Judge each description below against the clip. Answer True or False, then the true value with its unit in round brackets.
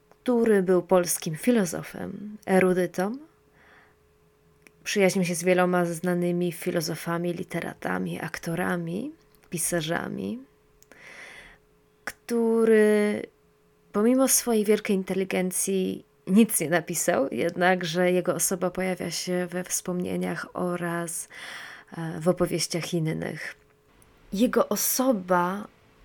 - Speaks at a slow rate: True (80 wpm)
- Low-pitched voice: False (180 Hz)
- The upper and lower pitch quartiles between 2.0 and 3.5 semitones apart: True (2.9 semitones)